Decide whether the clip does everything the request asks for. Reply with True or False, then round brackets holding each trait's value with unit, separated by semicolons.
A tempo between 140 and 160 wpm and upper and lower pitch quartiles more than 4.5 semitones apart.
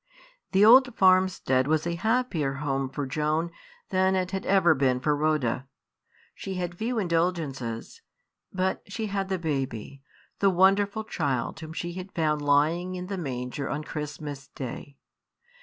True (150 wpm; 5.0 semitones)